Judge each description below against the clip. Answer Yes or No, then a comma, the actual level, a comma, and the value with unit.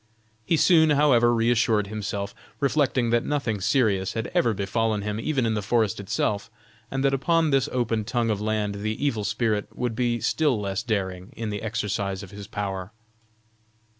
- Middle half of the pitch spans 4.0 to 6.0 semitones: No, average, 3.0 semitones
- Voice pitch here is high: No, low, 110 Hz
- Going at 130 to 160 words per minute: No, average, 170 wpm